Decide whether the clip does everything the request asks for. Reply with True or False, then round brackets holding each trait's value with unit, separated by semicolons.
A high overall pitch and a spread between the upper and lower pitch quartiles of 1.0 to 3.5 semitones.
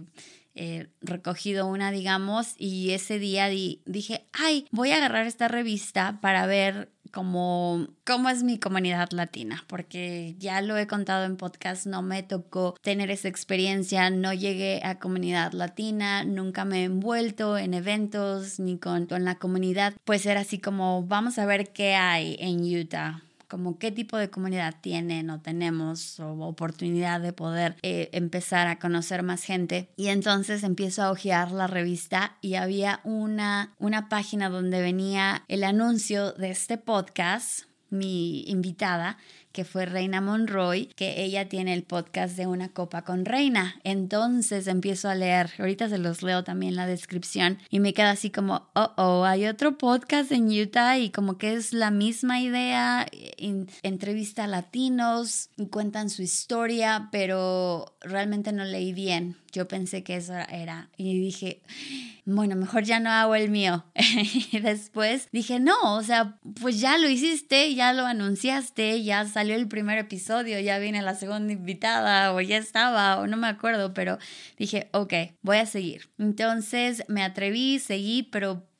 True (195 Hz; 2.8 semitones)